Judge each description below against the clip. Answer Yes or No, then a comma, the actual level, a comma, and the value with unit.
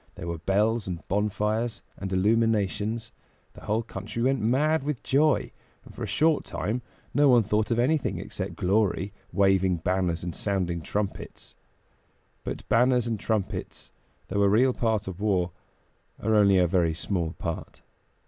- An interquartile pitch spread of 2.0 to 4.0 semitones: Yes, average, 3.6 semitones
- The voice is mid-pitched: No, low, 105 Hz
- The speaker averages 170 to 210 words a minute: No, average, 155 wpm